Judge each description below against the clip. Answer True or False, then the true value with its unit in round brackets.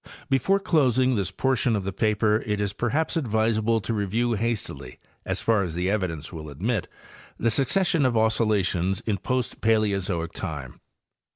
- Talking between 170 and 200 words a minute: False (160 wpm)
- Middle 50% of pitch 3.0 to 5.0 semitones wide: True (3.7 semitones)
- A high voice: False (110 Hz)